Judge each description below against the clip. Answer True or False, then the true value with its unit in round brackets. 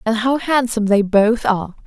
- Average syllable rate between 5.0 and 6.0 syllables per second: True (5.4 syllables/s)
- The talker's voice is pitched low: False (225 Hz)